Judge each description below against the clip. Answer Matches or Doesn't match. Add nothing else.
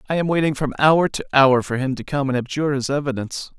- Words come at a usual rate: Doesn't match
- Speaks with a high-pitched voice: Doesn't match